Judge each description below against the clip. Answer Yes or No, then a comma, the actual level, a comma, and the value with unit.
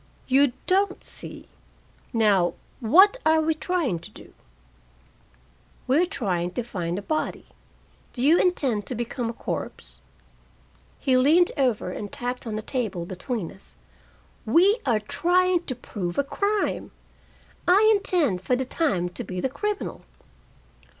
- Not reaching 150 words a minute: Yes, average, 140 wpm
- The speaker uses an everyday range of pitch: No, wide, 8.8 semitones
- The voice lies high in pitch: Yes, very high, 255 Hz